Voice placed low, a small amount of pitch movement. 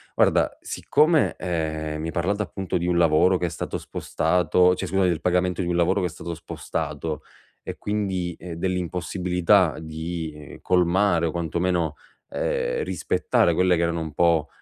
Yes: very low, 85 Hz; narrow, 2.2 semitones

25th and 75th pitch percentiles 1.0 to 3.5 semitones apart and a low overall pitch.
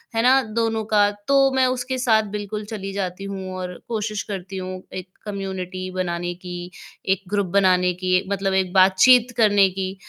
No: average, 2.8 semitones; high, 195 Hz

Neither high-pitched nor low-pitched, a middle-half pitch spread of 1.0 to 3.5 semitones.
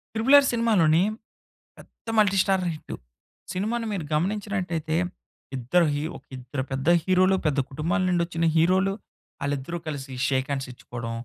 No: medium, 170 Hz; average, 5.3 semitones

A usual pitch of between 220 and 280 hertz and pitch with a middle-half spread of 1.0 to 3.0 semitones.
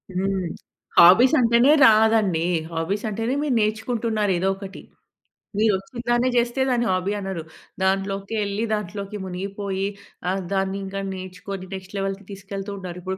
No: high, 195 Hz; narrow, 2.5 semitones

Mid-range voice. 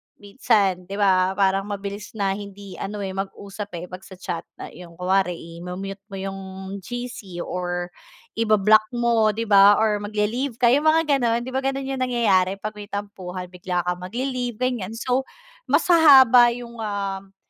No: high, 205 Hz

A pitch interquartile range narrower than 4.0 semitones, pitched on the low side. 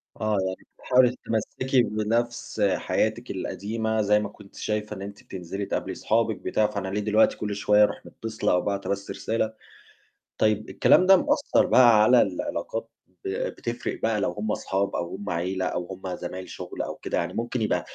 Yes: narrow, 2.5 semitones; low, 105 Hz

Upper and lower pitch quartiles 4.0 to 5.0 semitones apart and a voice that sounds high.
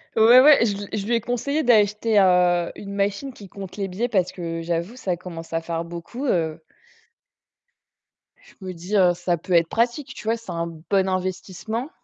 Yes: average, 4.6 semitones; high, 195 Hz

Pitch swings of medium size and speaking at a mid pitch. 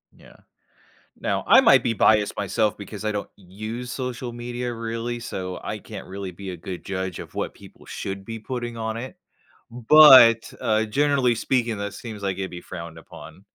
No: average, 3.5 semitones; low, 110 Hz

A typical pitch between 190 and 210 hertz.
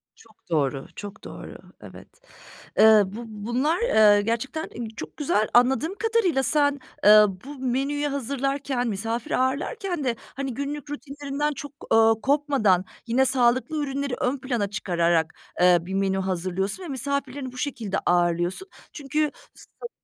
No: very high, 255 Hz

